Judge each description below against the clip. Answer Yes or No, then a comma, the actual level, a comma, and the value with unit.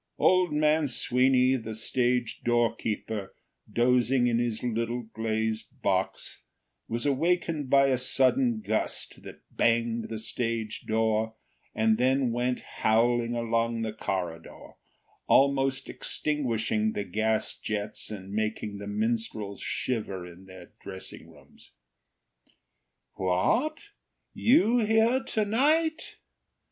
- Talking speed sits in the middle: No, slow, 110 wpm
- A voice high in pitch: No, low, 115 Hz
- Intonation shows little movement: No, average, 3.6 semitones